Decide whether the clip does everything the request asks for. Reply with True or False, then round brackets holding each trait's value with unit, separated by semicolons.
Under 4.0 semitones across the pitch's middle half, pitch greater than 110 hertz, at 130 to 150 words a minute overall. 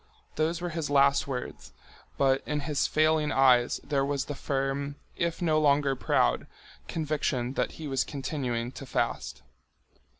True (2.4 semitones; 140 Hz; 145 wpm)